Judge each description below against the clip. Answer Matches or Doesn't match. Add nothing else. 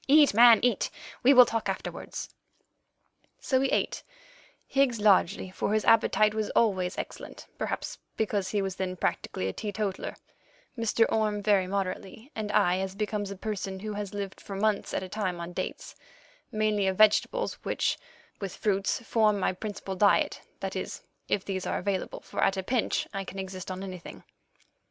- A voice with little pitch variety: Matches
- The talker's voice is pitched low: Doesn't match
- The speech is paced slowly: Doesn't match